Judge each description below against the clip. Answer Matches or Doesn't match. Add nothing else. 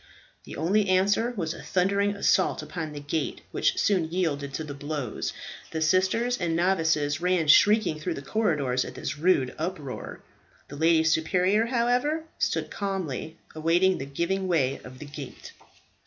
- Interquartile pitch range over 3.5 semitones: Matches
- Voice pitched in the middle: Matches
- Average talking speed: Matches